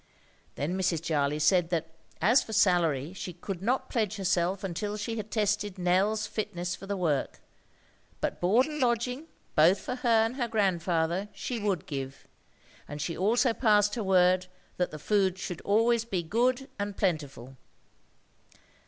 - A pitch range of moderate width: Yes, average, 4.1 semitones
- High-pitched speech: Yes, high, 195 Hz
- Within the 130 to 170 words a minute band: Yes, average, 160 wpm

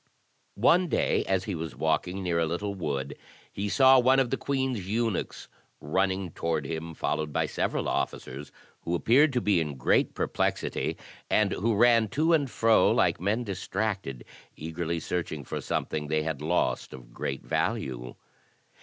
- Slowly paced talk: No, average, 160 wpm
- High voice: No, very low, 90 Hz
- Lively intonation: Yes, wide, 6.5 semitones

